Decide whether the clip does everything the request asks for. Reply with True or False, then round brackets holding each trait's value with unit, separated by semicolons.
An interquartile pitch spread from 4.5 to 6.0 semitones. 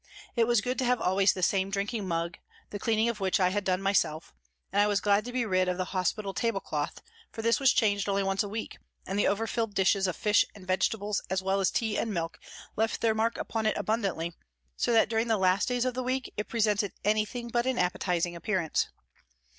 False (3.1 semitones)